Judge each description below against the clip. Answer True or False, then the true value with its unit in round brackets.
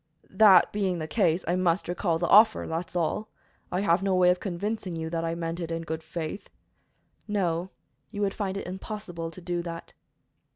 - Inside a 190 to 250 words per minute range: True (195 wpm)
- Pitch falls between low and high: True (175 Hz)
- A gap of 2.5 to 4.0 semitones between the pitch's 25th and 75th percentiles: True (2.9 semitones)